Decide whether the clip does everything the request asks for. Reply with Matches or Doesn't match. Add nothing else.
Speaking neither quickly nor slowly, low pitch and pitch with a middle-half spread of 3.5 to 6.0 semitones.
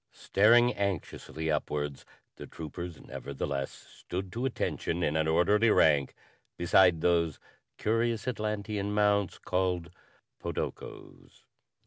Doesn't match